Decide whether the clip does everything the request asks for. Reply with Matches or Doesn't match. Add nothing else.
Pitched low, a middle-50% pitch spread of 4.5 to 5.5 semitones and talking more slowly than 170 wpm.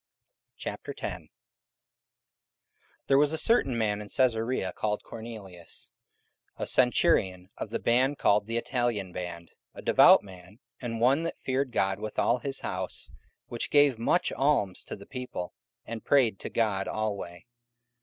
Matches